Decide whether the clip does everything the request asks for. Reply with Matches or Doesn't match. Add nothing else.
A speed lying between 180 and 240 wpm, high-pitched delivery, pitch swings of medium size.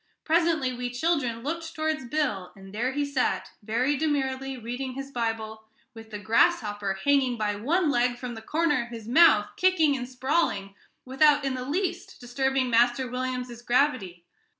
Doesn't match